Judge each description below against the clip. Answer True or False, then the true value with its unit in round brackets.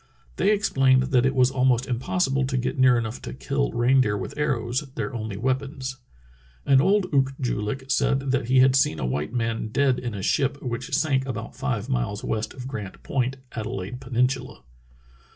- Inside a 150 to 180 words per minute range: False (190 wpm)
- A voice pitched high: False (130 Hz)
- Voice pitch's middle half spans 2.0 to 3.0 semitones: True (2.7 semitones)